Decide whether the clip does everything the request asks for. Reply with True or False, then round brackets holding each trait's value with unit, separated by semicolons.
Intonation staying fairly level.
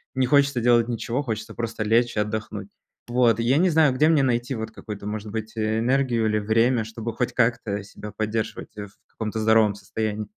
True (2.2 semitones)